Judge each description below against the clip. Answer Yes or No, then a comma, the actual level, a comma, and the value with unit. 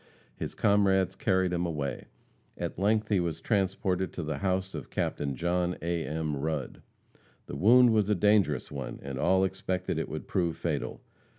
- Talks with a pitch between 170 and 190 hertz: No, very low, 90 Hz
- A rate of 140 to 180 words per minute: Yes, average, 170 wpm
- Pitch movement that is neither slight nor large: Yes, average, 3.4 semitones